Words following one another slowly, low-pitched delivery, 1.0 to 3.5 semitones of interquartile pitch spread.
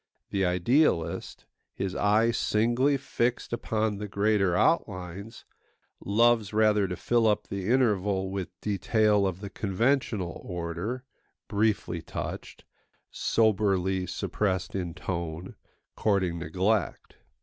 Yes: slow, 105 wpm; low, 100 Hz; average, 3.2 semitones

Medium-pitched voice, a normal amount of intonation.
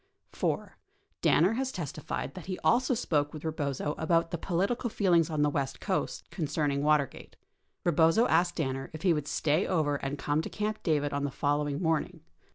Yes: medium, 160 Hz; average, 3.7 semitones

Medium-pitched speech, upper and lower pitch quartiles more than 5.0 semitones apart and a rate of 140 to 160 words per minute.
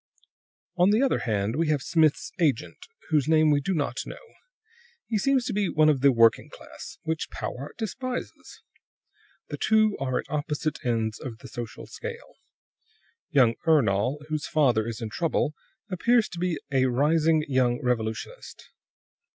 Yes: medium, 150 Hz; wide, 5.6 semitones; average, 155 wpm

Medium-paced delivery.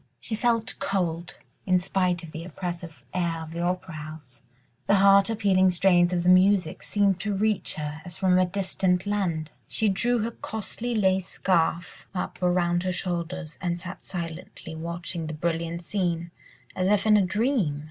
Yes: average, 170 wpm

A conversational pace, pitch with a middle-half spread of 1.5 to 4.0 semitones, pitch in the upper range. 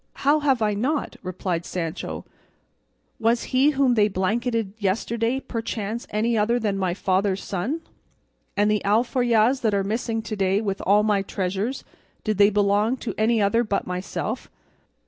Yes: average, 155 wpm; average, 3.0 semitones; high, 215 Hz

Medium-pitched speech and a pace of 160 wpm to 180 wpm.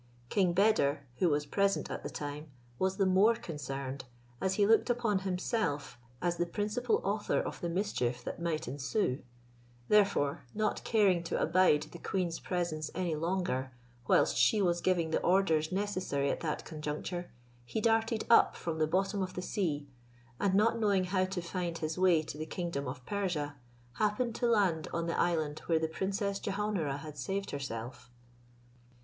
Yes: medium, 175 Hz; average, 170 wpm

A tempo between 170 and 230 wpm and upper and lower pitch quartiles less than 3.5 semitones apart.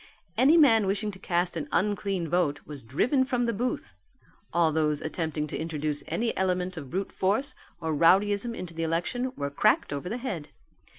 No: average, 180 wpm; average, 5.3 semitones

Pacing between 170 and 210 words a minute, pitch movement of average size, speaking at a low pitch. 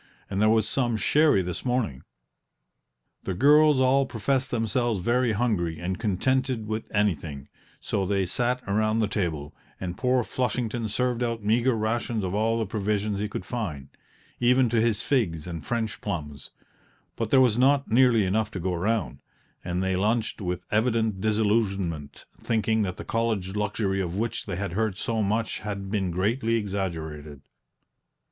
No: average, 160 wpm; average, 3.8 semitones; low, 110 Hz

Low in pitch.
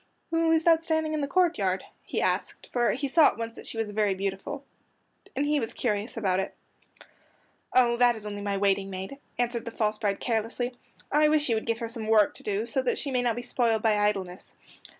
No: high, 230 Hz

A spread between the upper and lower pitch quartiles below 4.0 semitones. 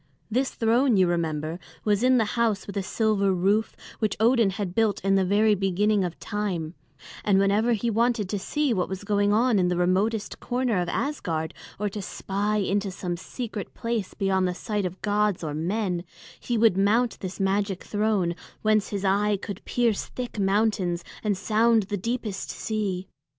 Yes: narrow, 2.6 semitones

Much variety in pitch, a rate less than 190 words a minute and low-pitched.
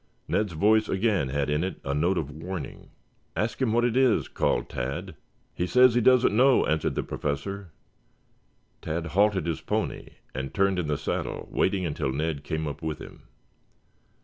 Yes: wide, 6.1 semitones; average, 175 wpm; very low, 90 Hz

